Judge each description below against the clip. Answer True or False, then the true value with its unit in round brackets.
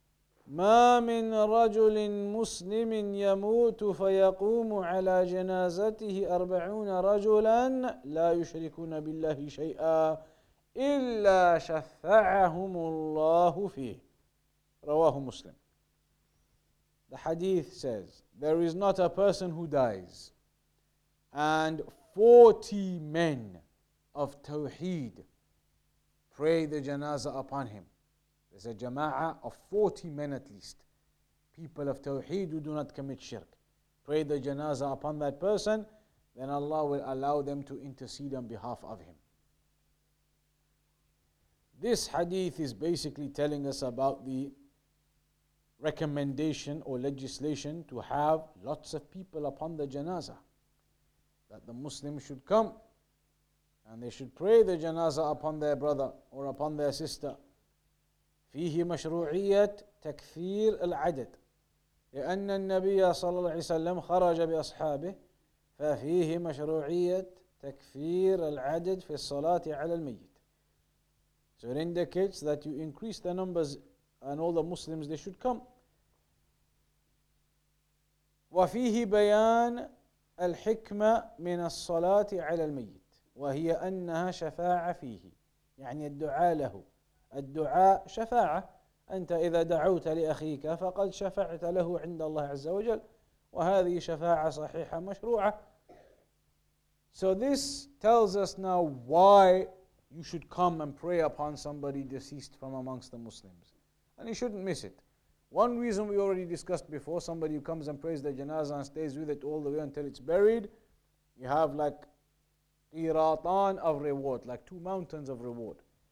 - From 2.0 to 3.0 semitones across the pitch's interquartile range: False (4.7 semitones)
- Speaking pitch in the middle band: True (160 Hz)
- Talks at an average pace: False (120 wpm)